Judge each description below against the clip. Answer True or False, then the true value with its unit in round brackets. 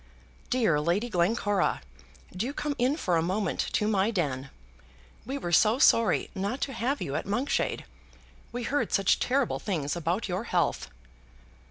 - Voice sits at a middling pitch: False (205 Hz)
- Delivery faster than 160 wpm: False (155 wpm)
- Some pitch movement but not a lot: False (5.8 semitones)